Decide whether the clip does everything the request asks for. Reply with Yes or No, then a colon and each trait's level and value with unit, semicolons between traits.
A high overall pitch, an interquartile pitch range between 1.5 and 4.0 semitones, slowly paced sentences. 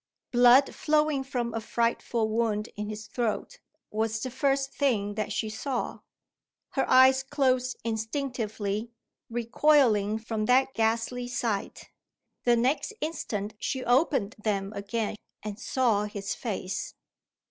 Yes: high, 235 Hz; average, 3.5 semitones; slow, 125 wpm